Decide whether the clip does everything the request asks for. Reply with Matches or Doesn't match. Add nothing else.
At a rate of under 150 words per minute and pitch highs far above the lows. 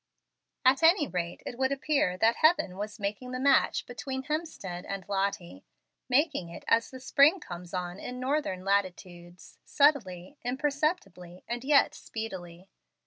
Matches